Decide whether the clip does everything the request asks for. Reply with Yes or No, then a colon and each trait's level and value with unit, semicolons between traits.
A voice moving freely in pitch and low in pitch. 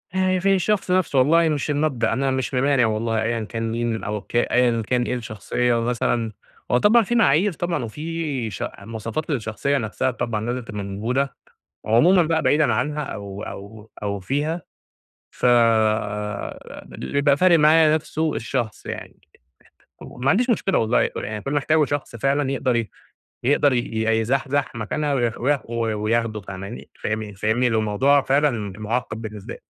No: average, 4.9 semitones; low, 125 Hz